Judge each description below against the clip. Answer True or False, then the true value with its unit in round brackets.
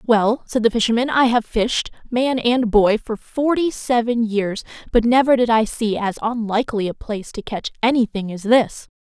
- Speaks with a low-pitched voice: False (230 Hz)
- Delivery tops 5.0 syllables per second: False (4.8 syllables/s)